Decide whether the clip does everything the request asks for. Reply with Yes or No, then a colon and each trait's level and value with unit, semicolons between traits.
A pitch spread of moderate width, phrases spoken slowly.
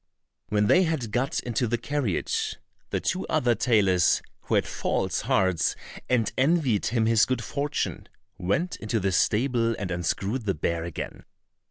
No: average, 4.7 semitones; average, 155 wpm